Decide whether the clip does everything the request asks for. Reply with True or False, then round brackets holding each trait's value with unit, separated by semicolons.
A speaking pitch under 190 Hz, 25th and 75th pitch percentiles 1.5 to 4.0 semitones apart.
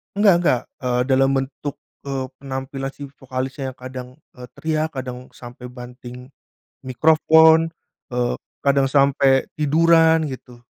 True (135 Hz; 3.5 semitones)